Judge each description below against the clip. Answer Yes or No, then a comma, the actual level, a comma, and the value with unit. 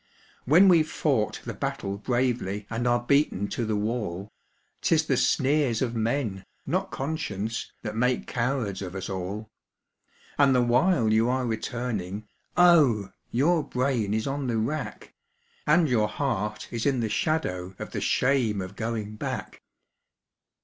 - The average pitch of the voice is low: Yes, low, 115 Hz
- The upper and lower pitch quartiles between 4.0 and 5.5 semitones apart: Yes, average, 4.4 semitones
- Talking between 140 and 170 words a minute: Yes, average, 150 wpm